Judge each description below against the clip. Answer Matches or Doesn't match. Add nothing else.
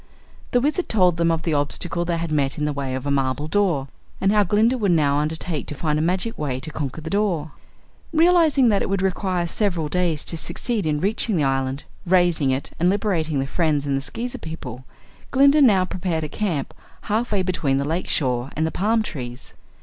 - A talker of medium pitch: Matches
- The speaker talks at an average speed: Doesn't match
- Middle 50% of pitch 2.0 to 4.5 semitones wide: Doesn't match